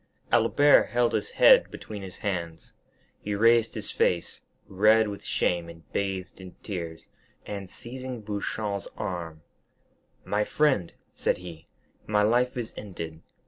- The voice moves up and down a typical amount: Yes, average, 4.1 semitones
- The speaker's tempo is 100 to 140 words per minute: Yes, slow, 135 wpm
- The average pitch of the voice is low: Yes, low, 100 Hz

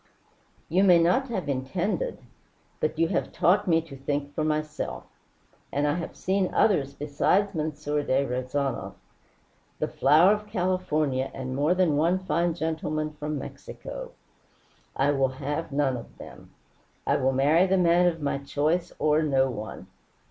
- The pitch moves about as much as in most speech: Yes, average, 4.0 semitones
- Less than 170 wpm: Yes, average, 155 wpm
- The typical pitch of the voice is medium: Yes, medium, 155 Hz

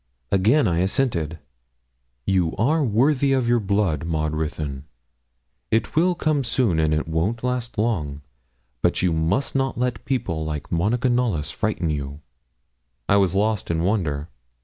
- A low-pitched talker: Yes, low, 100 Hz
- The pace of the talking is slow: No, average, 150 wpm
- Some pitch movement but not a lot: No, wide, 7.4 semitones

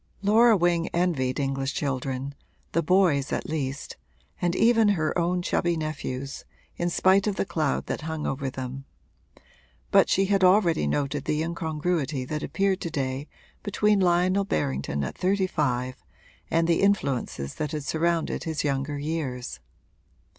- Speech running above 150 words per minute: No, average, 145 wpm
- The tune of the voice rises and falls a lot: No, average, 4.9 semitones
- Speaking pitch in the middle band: Yes, medium, 155 Hz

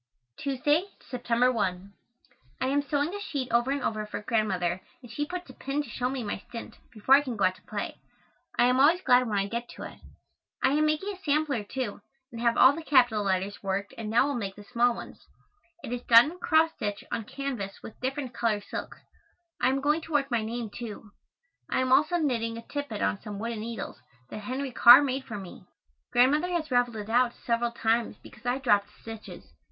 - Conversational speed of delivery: No, fast, 215 wpm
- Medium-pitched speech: No, high, 245 Hz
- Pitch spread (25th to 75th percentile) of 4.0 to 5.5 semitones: Yes, average, 4.4 semitones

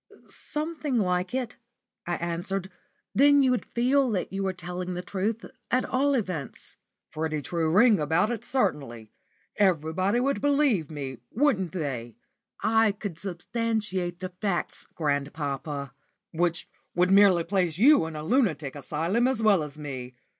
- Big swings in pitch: Yes, wide, 6.3 semitones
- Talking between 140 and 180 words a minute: Yes, average, 145 wpm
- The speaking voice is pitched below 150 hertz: No, medium, 185 Hz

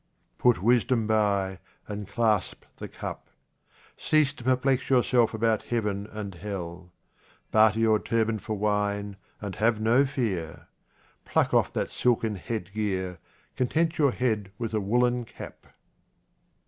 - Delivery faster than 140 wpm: No, slow, 135 wpm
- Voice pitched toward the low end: Yes, low, 110 Hz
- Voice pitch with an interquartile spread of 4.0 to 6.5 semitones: No, average, 3.1 semitones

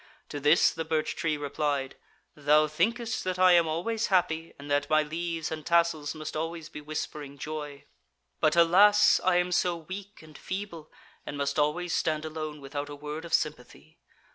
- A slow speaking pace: No, average, 175 wpm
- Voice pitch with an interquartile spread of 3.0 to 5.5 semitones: No, narrow, 2.5 semitones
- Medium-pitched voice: Yes, medium, 155 Hz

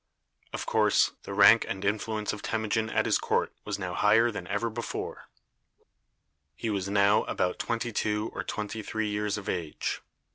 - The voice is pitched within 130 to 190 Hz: No, low, 105 Hz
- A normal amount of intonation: No, narrow, 1.7 semitones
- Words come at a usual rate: Yes, average, 170 wpm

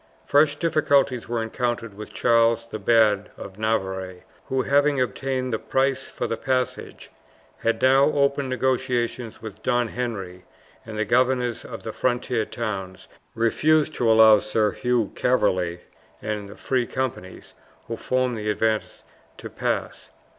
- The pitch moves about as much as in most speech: Yes, average, 3.2 semitones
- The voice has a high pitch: No, low, 115 Hz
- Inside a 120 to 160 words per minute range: Yes, average, 140 wpm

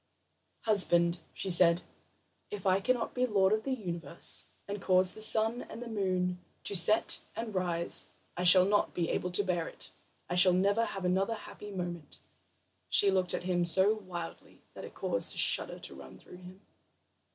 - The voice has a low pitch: No, medium, 185 Hz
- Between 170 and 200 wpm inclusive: Yes, average, 175 wpm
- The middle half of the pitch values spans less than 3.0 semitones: Yes, narrow, 2.6 semitones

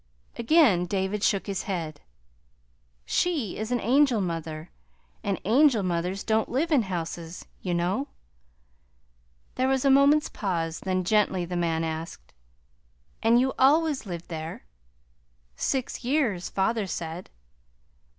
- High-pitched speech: Yes, high, 195 Hz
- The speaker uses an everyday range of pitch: No, wide, 6.8 semitones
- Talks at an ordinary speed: No, slow, 125 wpm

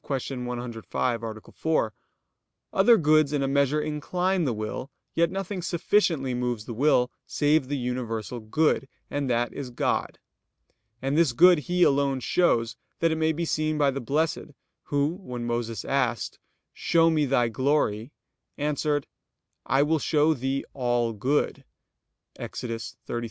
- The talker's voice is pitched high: No, medium, 140 Hz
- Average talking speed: Yes, average, 145 wpm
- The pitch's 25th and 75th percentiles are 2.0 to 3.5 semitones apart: No, average, 4.3 semitones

